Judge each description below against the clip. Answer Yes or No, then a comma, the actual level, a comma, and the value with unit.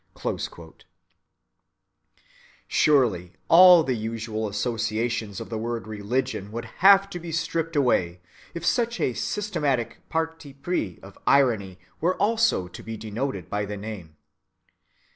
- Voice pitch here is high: No, low, 120 Hz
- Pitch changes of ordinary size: No, wide, 7.7 semitones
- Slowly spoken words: Yes, slow, 125 wpm